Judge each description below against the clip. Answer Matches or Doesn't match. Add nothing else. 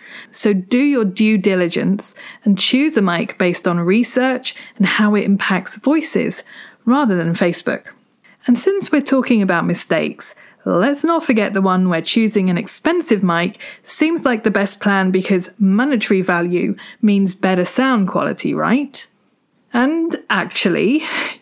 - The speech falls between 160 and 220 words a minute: Doesn't match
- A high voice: Matches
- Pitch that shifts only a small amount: Doesn't match